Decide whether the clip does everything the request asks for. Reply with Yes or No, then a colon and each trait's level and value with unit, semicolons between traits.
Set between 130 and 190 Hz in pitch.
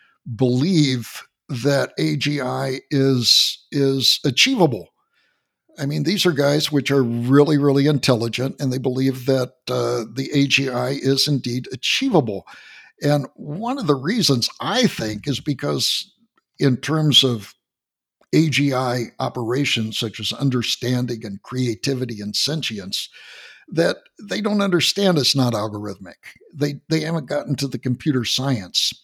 Yes: low, 135 Hz